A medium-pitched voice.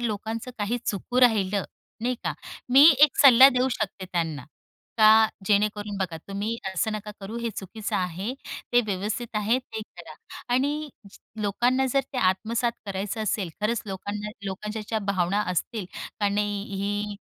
No: high, 210 Hz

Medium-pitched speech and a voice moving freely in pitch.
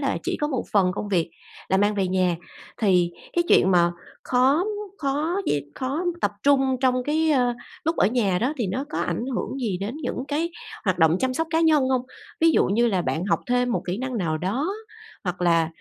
No: high, 245 Hz; wide, 6.8 semitones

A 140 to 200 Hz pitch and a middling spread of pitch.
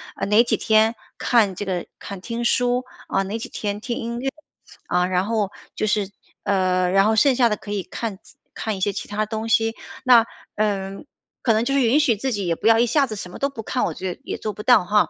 No: high, 215 Hz; average, 3.2 semitones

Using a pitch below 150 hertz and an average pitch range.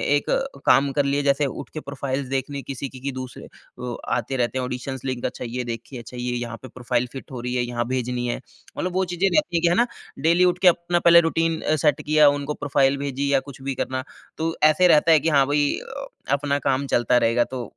Yes: medium, 140 Hz; average, 3.3 semitones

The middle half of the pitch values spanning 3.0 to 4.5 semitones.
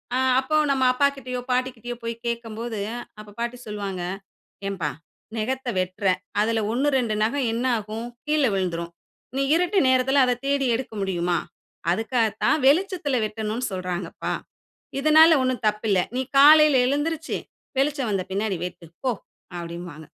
No: average, 5.1 semitones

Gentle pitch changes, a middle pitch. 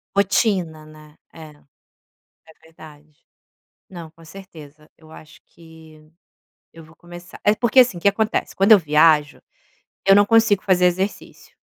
No: average, 4.1 semitones; medium, 165 Hz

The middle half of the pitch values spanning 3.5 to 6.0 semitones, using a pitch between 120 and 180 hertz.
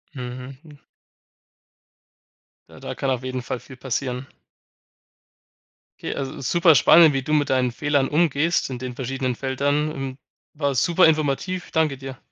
No: average, 2.7 semitones; low, 135 Hz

